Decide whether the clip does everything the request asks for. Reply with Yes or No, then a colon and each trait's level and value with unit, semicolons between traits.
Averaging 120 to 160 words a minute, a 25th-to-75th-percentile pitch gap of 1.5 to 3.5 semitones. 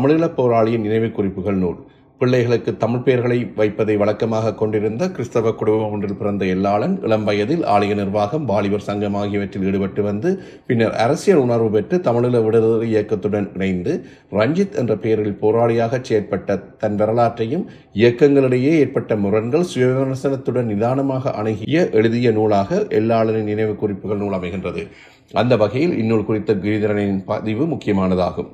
Yes: average, 125 wpm; average, 2.8 semitones